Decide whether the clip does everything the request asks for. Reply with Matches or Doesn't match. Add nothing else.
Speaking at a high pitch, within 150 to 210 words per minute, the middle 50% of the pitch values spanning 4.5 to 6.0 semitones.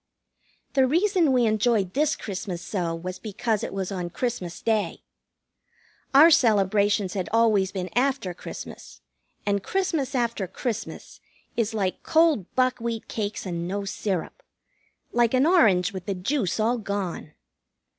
Doesn't match